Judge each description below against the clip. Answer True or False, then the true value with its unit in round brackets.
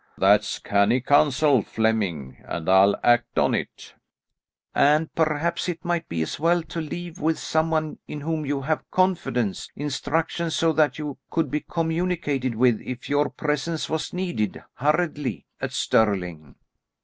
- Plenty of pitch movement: True (6.0 semitones)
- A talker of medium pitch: True (150 Hz)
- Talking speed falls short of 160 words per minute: True (150 wpm)